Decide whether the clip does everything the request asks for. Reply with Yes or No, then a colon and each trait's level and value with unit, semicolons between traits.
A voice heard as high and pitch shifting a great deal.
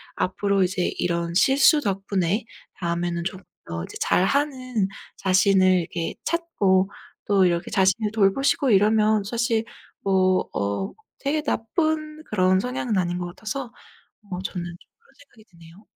No: high, 195 Hz; average, 4.4 semitones